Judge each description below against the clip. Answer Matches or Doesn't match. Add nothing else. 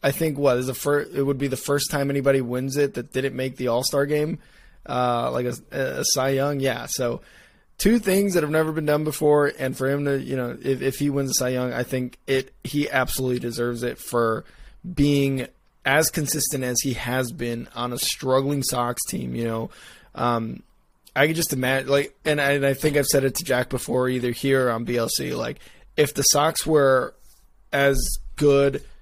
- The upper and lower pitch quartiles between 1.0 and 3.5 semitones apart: Matches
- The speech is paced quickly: Matches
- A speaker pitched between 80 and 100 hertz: Doesn't match